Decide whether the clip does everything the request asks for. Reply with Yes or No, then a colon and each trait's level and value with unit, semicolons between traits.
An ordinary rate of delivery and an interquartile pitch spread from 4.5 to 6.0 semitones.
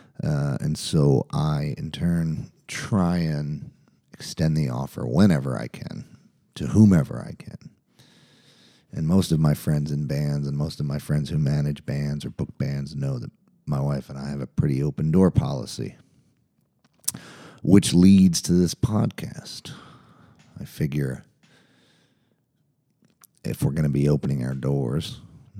Yes: average, 150 wpm; average, 4.9 semitones